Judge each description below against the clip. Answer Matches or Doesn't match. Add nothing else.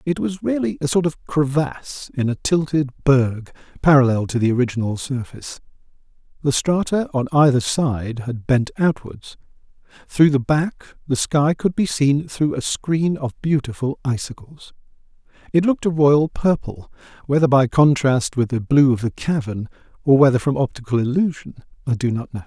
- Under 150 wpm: Doesn't match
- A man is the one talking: Matches